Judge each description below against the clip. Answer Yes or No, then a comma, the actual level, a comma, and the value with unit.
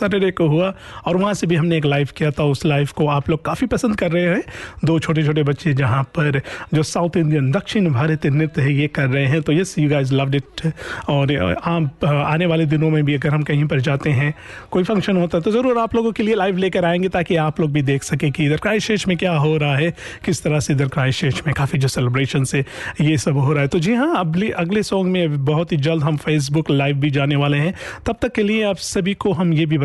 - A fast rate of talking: Yes, fast, 255 wpm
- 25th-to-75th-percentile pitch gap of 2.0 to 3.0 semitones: No, average, 3.8 semitones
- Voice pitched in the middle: Yes, medium, 155 Hz